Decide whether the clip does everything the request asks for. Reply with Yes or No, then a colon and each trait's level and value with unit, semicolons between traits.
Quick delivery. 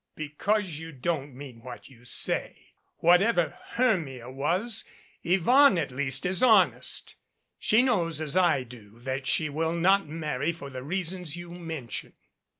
No: average, 145 wpm